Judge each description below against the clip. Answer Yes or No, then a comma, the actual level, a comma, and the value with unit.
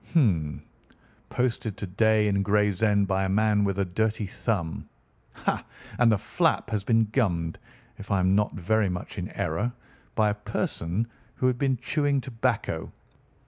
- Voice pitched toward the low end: Yes, low, 105 Hz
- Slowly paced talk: No, average, 160 wpm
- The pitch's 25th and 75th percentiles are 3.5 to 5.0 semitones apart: No, average, 2.9 semitones